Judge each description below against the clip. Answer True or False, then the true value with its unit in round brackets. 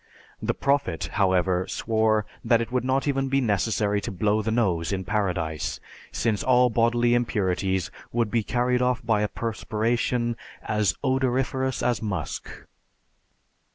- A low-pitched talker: True (110 Hz)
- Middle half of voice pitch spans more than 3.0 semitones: True (3.4 semitones)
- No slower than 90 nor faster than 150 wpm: True (140 wpm)